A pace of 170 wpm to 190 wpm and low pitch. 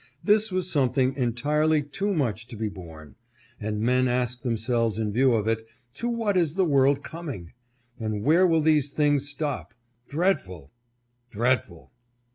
No: average, 150 wpm; low, 130 Hz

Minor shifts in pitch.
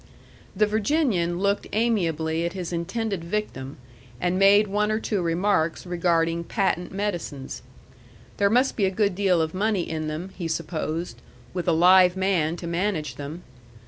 No: average, 3.5 semitones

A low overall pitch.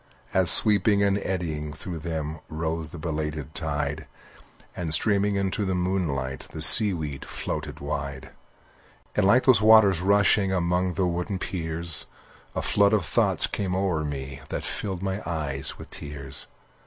Yes: very low, 85 Hz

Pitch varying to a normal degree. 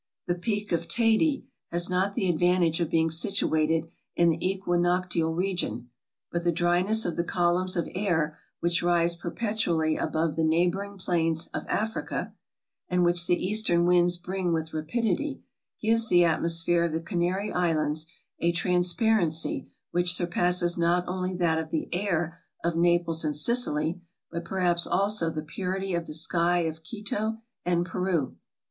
No: narrow, 2.1 semitones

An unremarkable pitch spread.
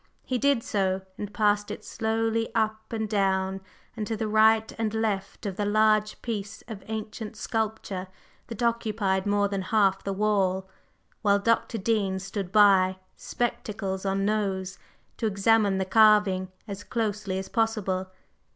No: narrow, 2.3 semitones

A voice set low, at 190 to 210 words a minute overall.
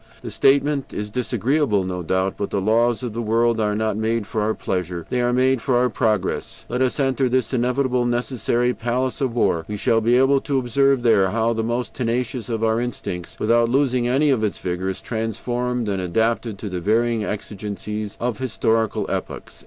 Yes: low, 115 Hz; average, 195 wpm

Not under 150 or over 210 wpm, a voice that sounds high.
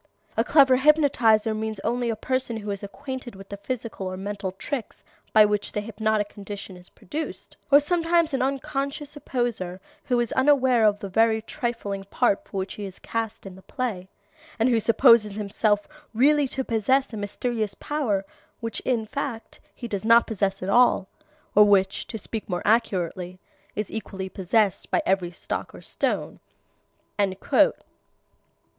Yes: average, 160 wpm; high, 220 Hz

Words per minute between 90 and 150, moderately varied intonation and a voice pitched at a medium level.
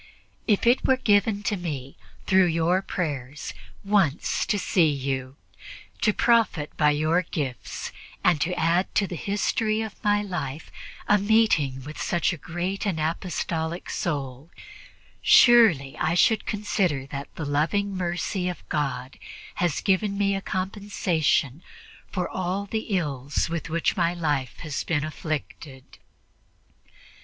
Yes: slow, 135 wpm; average, 5.0 semitones; medium, 170 Hz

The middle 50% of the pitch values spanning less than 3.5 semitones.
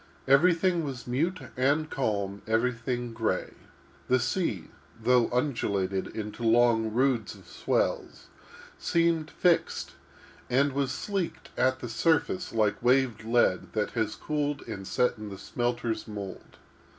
No: average, 4.3 semitones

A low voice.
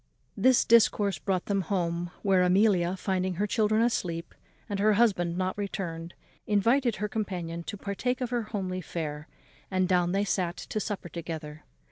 No: high, 190 Hz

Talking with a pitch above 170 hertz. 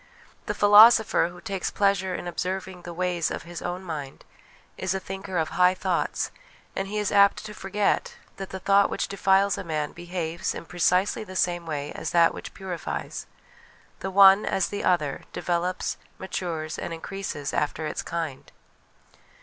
Yes: medium, 185 Hz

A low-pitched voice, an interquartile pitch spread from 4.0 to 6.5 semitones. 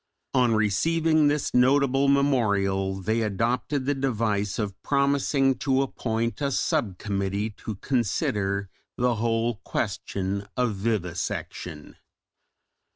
Yes: low, 115 Hz; average, 5.1 semitones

